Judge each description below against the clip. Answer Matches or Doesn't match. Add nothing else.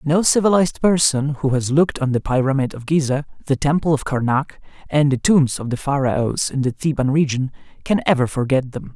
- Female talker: Doesn't match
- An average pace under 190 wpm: Doesn't match